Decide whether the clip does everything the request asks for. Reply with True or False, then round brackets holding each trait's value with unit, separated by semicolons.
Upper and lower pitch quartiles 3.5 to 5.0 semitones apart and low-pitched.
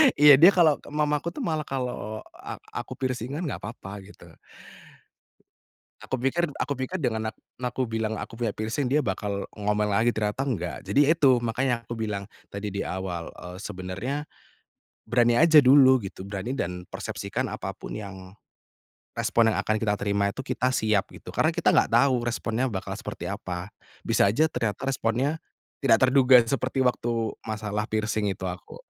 True (4.4 semitones; 115 Hz)